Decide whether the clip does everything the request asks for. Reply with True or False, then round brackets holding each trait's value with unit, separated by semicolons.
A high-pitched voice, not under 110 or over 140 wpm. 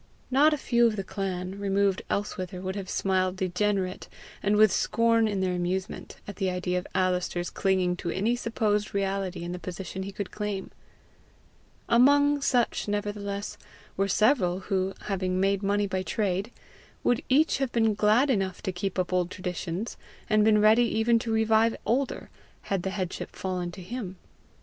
False (195 Hz; 170 wpm)